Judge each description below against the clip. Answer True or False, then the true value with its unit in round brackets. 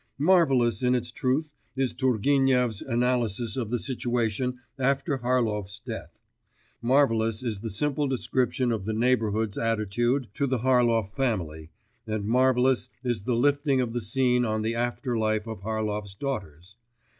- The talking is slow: False (145 wpm)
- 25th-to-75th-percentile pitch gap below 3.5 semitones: True (3.0 semitones)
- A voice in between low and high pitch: False (120 Hz)